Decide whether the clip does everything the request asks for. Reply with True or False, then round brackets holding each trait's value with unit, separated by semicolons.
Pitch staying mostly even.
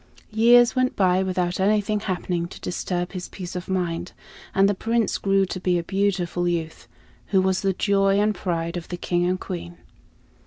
True (2.2 semitones)